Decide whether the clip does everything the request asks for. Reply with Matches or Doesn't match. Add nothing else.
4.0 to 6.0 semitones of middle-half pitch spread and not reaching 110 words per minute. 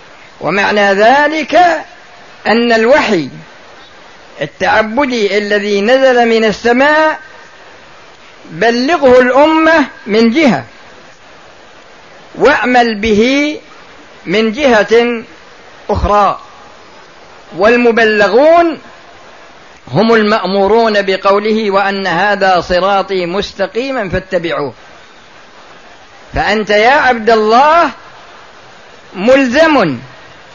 Matches